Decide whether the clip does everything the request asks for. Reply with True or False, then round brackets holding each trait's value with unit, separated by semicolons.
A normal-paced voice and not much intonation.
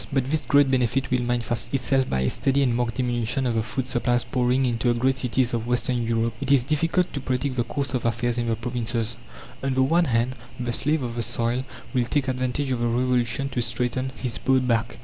False (230 wpm; 2.0 semitones)